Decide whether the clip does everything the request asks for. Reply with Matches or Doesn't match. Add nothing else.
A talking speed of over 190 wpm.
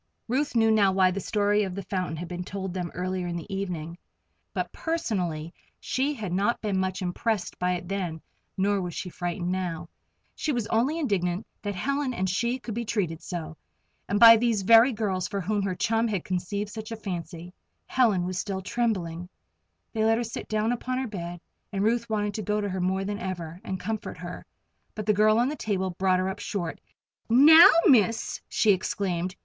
Matches